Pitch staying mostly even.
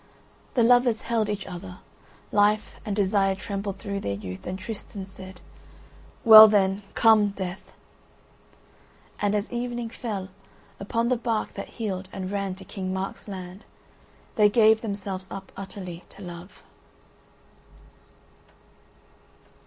Yes: narrow, 2.3 semitones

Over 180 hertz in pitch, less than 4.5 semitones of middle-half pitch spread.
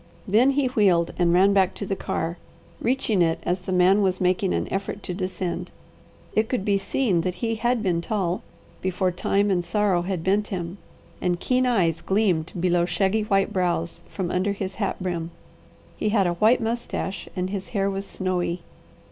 Yes: high, 190 Hz; narrow, 2.6 semitones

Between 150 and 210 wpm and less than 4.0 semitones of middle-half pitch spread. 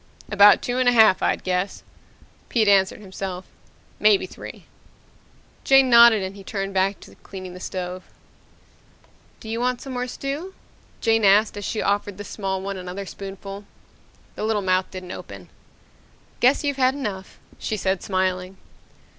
Yes: average, 155 wpm; average, 3.3 semitones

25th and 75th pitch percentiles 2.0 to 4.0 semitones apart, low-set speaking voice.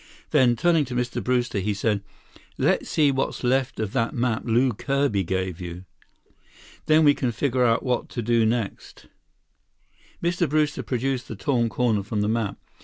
Yes: average, 3.7 semitones; low, 120 Hz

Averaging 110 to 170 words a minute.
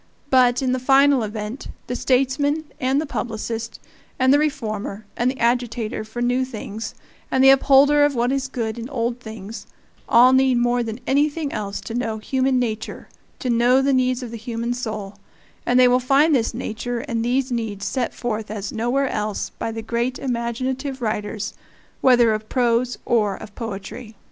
No: average, 180 wpm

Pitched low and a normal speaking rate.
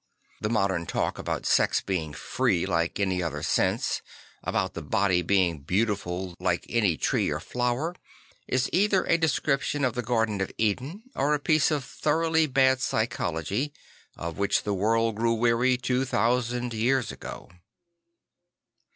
Yes: low, 115 Hz; average, 150 wpm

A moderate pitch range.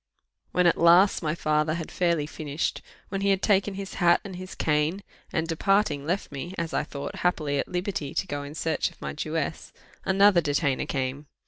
Yes: average, 4.0 semitones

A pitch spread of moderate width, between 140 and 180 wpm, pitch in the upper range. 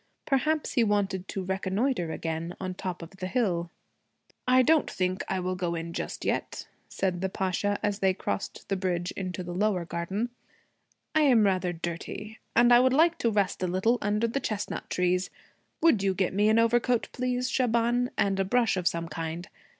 No: average, 4.5 semitones; average, 190 wpm; high, 195 Hz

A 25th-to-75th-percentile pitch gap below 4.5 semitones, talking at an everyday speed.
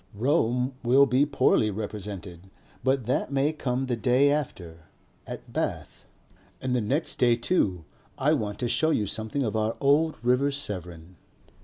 No: average, 4.8 semitones; average, 155 wpm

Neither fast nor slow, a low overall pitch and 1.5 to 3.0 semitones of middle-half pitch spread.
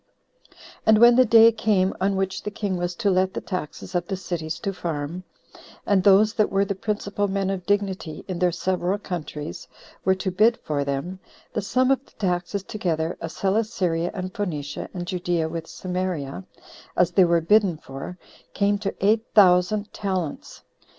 No: average, 175 wpm; medium, 185 Hz; average, 2.7 semitones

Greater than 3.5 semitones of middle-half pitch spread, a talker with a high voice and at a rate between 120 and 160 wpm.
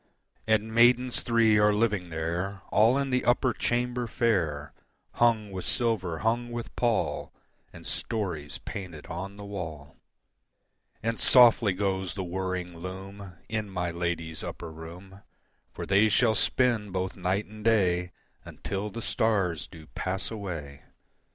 No: average, 4.2 semitones; low, 100 Hz; average, 140 wpm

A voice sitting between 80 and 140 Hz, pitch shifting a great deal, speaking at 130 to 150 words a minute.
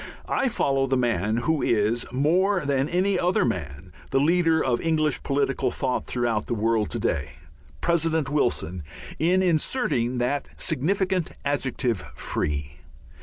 Yes: low, 135 Hz; wide, 5.8 semitones; slow, 135 wpm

